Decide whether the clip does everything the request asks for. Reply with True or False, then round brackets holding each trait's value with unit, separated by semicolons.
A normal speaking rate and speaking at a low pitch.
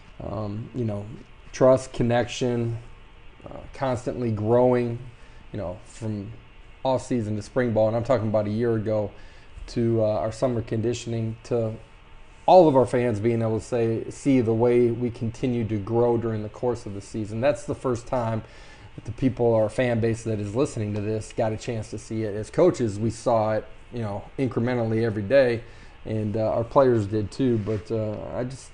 True (190 wpm; 115 Hz)